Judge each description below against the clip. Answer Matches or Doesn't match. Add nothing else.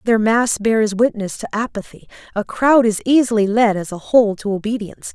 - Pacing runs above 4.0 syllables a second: Matches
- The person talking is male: Doesn't match